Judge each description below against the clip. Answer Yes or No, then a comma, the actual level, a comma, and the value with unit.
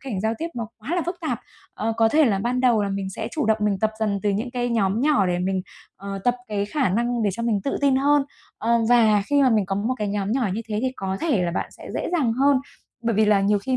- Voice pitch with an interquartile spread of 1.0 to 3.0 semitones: No, average, 4.2 semitones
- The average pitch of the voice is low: No, high, 225 Hz